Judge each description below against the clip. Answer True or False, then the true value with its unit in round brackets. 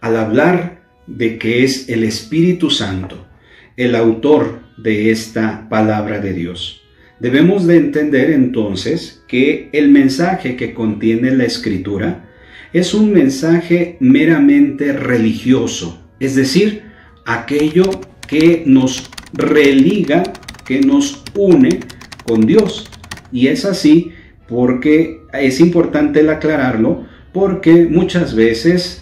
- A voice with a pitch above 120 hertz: True (135 Hz)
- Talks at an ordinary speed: False (110 wpm)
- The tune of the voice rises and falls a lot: True (6.9 semitones)